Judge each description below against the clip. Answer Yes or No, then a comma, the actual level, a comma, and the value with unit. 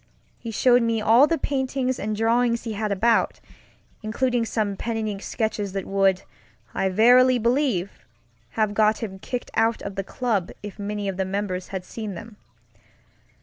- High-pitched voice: Yes, high, 220 Hz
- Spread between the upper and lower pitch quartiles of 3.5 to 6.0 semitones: No, average, 3.0 semitones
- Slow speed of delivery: No, average, 170 wpm